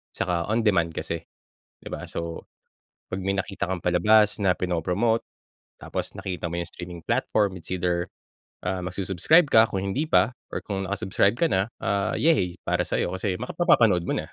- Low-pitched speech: Yes, very low, 95 Hz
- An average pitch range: Yes, average, 3.1 semitones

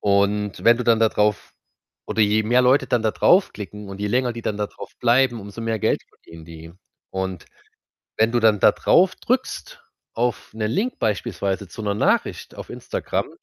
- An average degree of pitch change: Yes, average, 3.0 semitones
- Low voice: Yes, low, 110 Hz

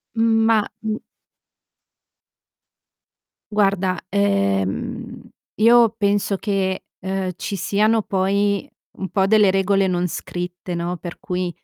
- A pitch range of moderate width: No, narrow, 2.3 semitones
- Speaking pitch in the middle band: No, high, 195 Hz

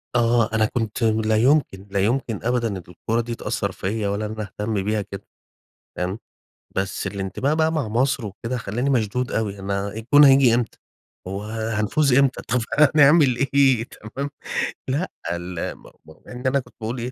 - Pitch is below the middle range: Yes, low, 115 Hz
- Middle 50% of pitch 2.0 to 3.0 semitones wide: No, average, 3.7 semitones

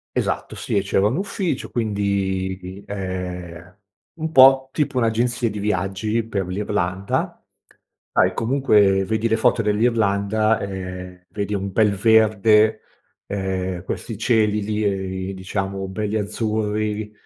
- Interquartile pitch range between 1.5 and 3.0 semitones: Yes, narrow, 2.5 semitones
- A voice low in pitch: Yes, low, 105 Hz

